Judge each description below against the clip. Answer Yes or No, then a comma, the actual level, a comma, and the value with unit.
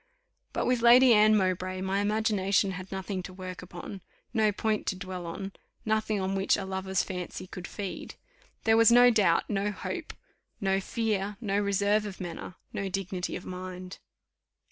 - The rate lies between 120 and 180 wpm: Yes, average, 165 wpm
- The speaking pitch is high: Yes, high, 195 Hz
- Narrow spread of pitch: Yes, narrow, 2.2 semitones